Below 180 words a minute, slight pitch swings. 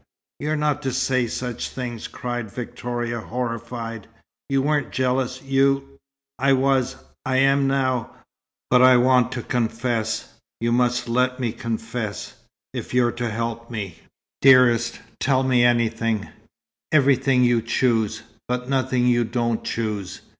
Yes: slow, 135 wpm; narrow, 2.1 semitones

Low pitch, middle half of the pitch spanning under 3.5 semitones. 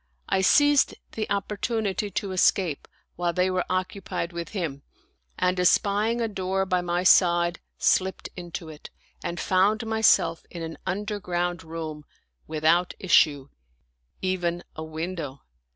No: medium, 180 Hz; narrow, 2.5 semitones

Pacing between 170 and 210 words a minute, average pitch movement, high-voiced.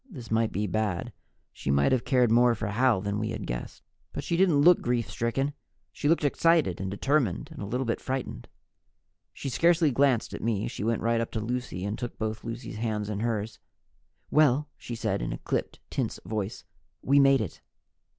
No: average, 200 wpm; average, 4.2 semitones; low, 115 Hz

